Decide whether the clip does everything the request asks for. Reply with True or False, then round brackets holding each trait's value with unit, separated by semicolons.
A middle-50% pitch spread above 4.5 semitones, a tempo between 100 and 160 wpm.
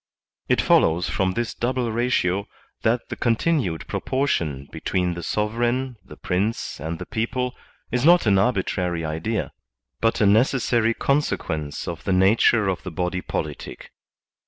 True (5.2 semitones; 145 wpm)